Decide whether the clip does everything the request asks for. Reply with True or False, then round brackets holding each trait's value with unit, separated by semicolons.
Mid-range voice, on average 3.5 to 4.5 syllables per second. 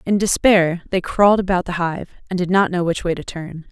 False (180 Hz; 5.5 syllables/s)